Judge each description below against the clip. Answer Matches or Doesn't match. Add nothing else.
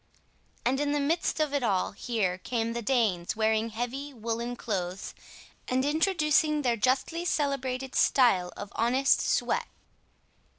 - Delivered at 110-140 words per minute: Matches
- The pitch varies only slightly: Doesn't match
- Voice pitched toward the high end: Matches